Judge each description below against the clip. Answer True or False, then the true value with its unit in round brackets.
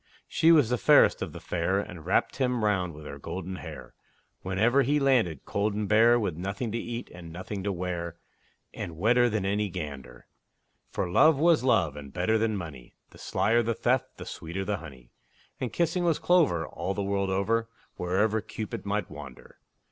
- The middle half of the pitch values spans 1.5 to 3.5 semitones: False (5.2 semitones)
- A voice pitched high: False (100 Hz)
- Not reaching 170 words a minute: False (185 wpm)